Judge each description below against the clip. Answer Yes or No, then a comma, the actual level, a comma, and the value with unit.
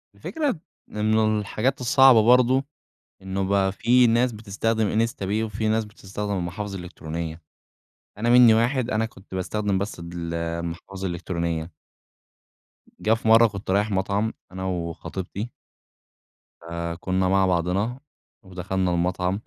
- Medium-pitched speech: No, low, 100 Hz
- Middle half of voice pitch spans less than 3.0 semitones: No, average, 3.7 semitones